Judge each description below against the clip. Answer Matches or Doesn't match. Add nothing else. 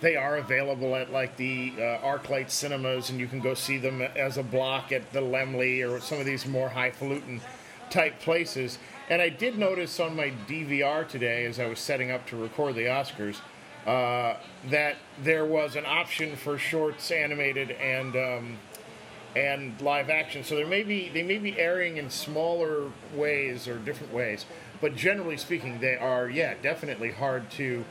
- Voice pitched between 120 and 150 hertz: Matches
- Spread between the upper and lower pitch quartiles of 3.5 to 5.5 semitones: Doesn't match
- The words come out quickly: Doesn't match